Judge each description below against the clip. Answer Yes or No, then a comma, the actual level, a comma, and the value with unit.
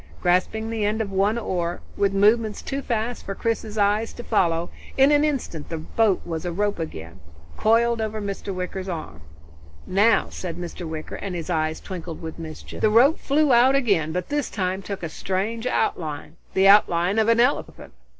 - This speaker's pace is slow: No, average, 185 wpm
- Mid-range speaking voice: No, high, 200 Hz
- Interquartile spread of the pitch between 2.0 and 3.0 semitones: No, average, 4.8 semitones